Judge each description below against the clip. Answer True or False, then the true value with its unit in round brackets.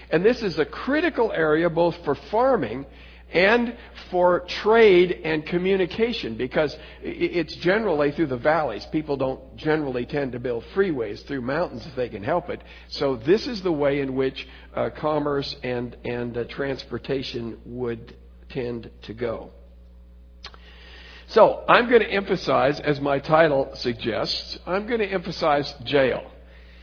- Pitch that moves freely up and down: True (6.6 semitones)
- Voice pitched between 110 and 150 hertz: True (140 Hz)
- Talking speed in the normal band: True (145 wpm)